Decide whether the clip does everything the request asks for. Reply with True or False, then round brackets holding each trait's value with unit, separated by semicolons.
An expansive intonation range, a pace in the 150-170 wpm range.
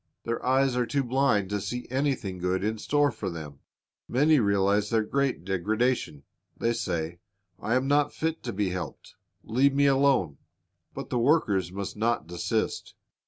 True (6.0 semitones; 165 wpm)